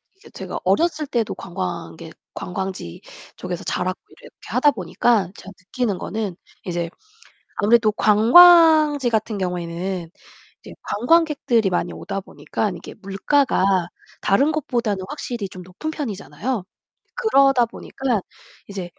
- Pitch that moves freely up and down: Yes, wide, 6.8 semitones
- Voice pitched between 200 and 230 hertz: Yes, high, 215 Hz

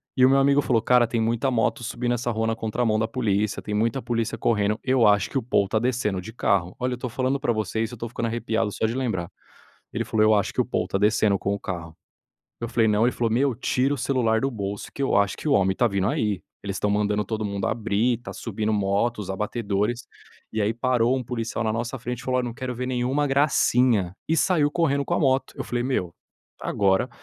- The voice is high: No, low, 115 Hz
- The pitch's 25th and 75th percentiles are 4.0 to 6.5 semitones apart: No, average, 3.2 semitones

